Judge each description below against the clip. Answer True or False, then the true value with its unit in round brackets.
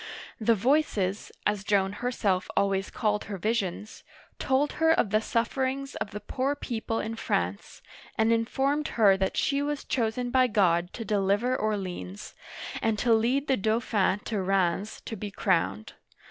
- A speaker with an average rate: True (160 wpm)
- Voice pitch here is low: False (215 Hz)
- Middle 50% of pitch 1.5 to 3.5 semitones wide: False (4.2 semitones)